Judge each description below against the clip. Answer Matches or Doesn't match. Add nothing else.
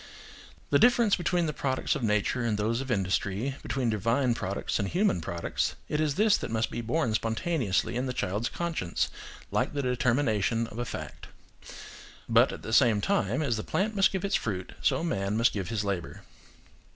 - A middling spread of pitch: Doesn't match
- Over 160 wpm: Matches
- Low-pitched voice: Matches